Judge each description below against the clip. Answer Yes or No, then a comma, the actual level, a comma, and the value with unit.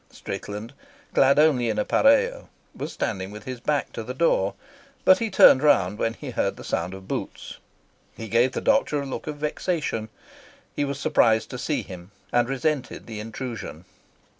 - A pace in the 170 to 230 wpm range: Yes, average, 175 wpm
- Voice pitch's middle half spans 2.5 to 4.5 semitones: No, wide, 5.5 semitones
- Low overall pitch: Yes, low, 125 Hz